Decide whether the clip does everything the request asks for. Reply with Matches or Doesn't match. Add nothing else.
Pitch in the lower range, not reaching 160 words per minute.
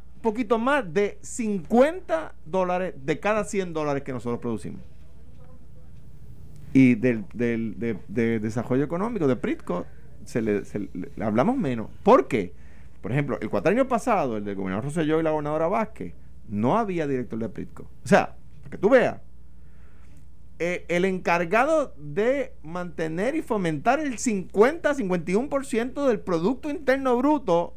Doesn't match